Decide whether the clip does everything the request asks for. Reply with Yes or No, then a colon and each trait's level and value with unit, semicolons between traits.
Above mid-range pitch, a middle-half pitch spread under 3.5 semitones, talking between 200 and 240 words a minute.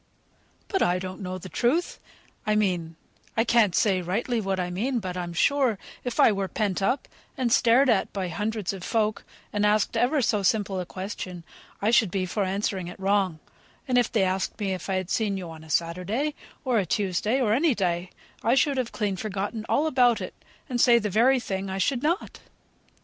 No: high, 205 Hz; average, 4.2 semitones; fast, 205 wpm